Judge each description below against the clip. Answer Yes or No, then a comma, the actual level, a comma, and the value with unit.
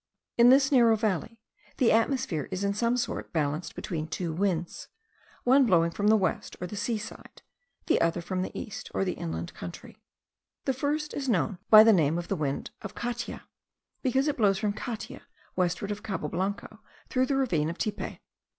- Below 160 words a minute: No, average, 185 wpm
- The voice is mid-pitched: No, high, 205 Hz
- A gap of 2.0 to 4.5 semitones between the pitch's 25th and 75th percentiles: No, wide, 5.6 semitones